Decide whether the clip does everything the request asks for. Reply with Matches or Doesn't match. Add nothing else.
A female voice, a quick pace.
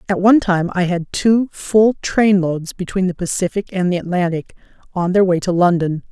Doesn't match